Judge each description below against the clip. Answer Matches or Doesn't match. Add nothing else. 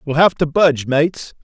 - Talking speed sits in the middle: Doesn't match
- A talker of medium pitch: Matches